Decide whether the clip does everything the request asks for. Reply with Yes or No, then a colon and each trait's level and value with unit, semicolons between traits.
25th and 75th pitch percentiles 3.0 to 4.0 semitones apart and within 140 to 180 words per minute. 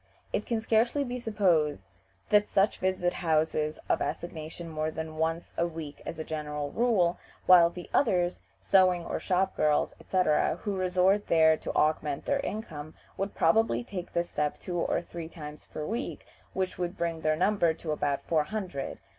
Yes: average, 3.6 semitones; average, 170 wpm